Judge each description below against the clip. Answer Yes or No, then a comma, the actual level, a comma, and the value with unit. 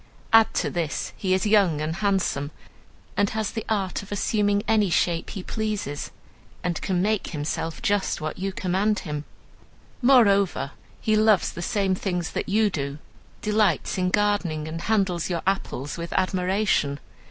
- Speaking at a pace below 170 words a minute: Yes, average, 155 wpm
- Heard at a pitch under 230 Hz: Yes, high, 190 Hz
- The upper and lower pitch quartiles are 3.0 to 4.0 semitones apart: Yes, average, 3.6 semitones